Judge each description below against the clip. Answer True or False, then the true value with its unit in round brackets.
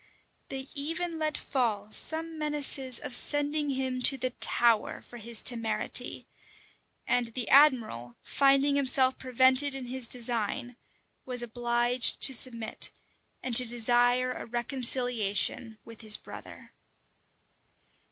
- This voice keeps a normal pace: False (120 wpm)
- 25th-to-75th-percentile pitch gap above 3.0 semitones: False (2.5 semitones)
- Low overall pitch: False (250 Hz)